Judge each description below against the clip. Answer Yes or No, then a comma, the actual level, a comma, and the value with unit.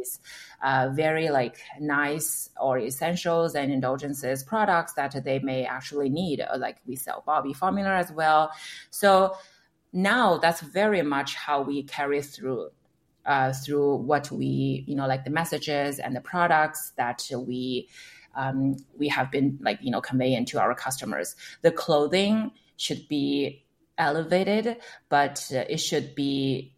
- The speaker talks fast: No, average, 145 wpm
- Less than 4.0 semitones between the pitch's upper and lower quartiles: Yes, average, 3.3 semitones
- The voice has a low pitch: No, medium, 145 Hz